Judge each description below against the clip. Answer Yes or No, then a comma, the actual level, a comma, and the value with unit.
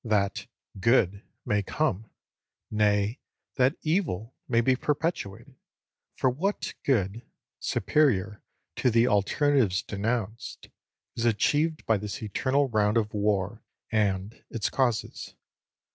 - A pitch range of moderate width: Yes, average, 4.2 semitones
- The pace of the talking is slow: Yes, slow, 110 wpm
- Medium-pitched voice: No, low, 110 Hz